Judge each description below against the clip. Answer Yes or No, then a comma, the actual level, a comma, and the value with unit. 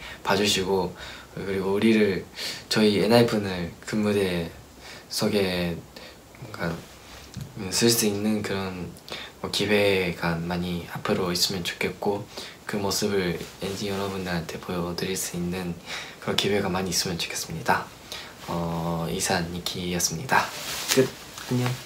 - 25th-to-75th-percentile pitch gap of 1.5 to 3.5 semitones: Yes, average, 2.9 semitones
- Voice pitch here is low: Yes, very low, 95 Hz